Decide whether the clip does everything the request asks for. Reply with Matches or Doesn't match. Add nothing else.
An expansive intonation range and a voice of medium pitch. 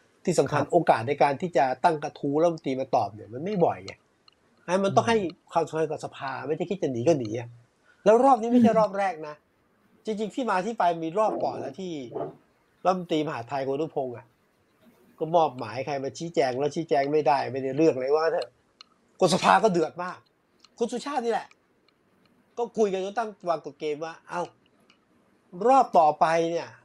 Matches